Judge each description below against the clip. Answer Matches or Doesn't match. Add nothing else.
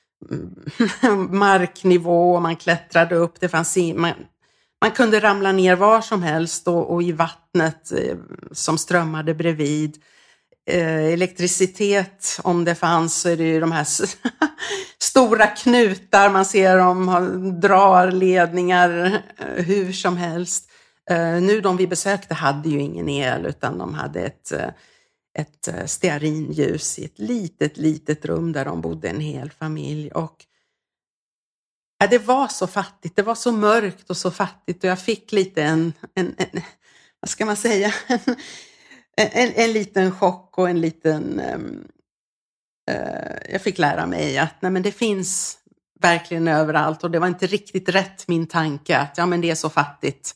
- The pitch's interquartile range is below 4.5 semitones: Matches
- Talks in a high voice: Doesn't match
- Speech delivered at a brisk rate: Doesn't match